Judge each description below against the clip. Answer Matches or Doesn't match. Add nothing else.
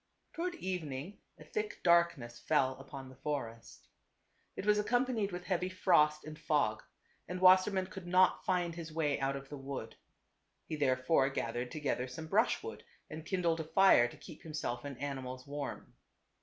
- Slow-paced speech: Doesn't match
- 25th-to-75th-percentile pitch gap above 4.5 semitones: Matches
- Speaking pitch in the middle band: Matches